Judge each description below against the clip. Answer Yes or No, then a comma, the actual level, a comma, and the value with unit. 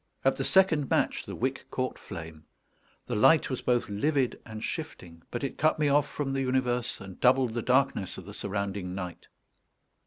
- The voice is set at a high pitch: No, low, 125 Hz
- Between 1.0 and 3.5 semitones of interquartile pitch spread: No, average, 5.3 semitones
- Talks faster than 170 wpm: Yes, average, 185 wpm